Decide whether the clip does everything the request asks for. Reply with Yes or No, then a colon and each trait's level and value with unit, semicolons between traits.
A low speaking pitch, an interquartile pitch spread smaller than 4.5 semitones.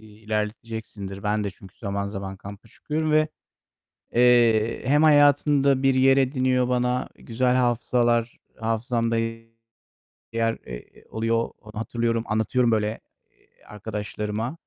Yes: low, 115 Hz; average, 2.9 semitones